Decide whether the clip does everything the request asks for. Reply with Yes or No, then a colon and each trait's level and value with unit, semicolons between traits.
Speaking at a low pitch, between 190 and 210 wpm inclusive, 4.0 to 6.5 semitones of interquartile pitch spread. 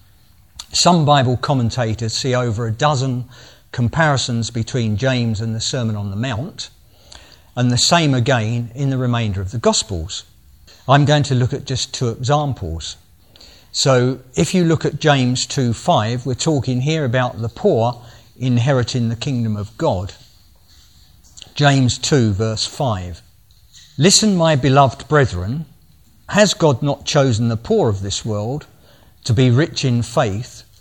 No: low, 125 Hz; average, 140 wpm; average, 4.5 semitones